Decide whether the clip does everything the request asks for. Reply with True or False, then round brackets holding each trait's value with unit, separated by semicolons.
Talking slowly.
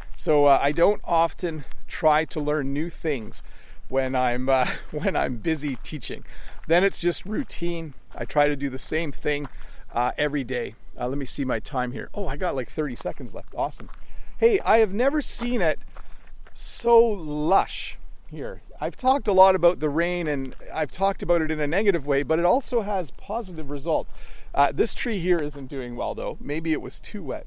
False (195 wpm)